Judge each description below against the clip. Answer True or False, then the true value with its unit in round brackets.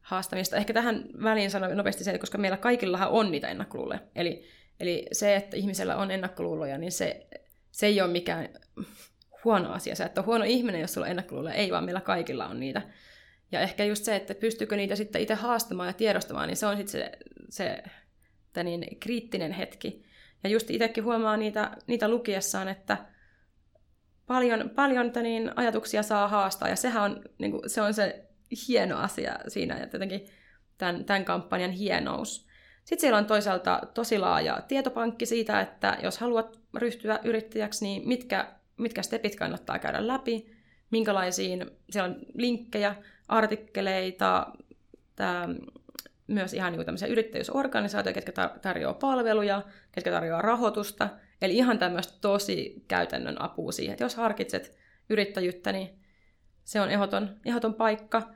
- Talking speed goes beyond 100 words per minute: True (150 wpm)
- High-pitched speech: True (215 Hz)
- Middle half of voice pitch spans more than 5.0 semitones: False (2.9 semitones)